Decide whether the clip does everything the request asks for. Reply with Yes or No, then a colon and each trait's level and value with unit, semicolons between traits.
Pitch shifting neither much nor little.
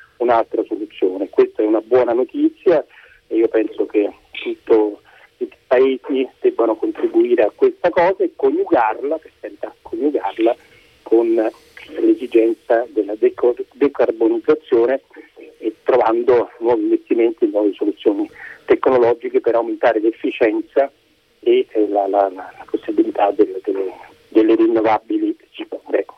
Yes: average, 3.6 semitones